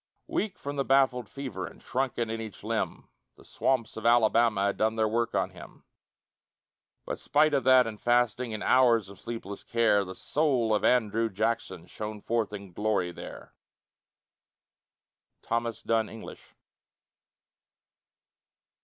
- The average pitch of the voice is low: Yes, low, 115 Hz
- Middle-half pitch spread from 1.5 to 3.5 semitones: Yes, average, 2.7 semitones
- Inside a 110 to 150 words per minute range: Yes, average, 140 wpm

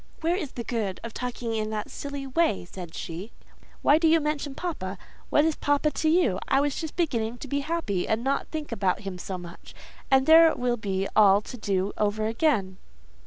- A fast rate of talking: Yes, fast, 210 wpm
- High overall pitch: Yes, high, 240 Hz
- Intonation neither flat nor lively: No, wide, 6.9 semitones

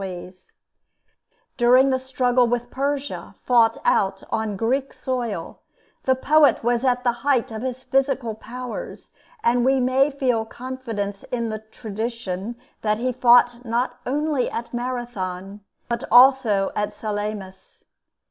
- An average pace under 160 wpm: Yes, slow, 135 wpm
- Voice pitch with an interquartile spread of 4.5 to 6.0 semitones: No, average, 3.0 semitones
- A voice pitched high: Yes, high, 240 Hz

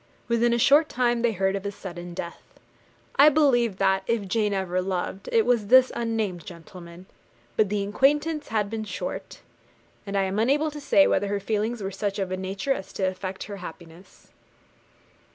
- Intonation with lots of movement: No, average, 4.0 semitones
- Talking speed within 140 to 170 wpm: No, average, 185 wpm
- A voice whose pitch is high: Yes, high, 205 Hz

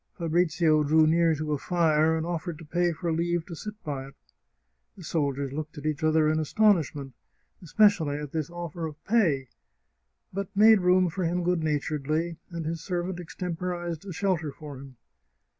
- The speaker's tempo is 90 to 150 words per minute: No, average, 175 wpm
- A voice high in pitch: No, medium, 165 Hz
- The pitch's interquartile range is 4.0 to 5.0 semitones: No, narrow, 2.4 semitones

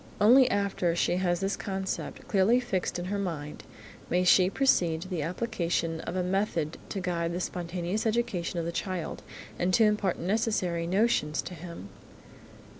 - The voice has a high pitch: No, medium, 180 Hz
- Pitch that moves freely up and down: No, average, 3.0 semitones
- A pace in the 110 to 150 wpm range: No, average, 165 wpm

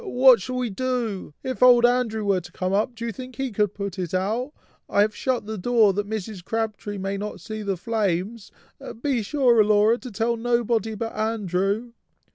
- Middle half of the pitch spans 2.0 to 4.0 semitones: Yes, average, 3.2 semitones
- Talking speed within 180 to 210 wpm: Yes, average, 195 wpm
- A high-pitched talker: Yes, high, 220 Hz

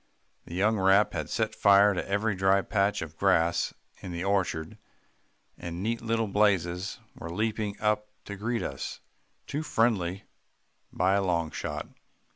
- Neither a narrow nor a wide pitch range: Yes, average, 3.1 semitones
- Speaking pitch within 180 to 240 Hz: No, low, 100 Hz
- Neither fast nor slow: Yes, average, 150 wpm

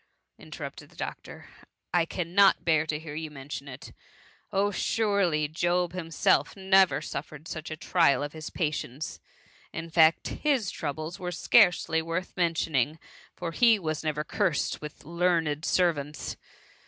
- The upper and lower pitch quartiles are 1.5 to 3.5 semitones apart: Yes, average, 2.9 semitones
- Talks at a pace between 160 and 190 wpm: No, average, 145 wpm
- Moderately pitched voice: Yes, medium, 165 Hz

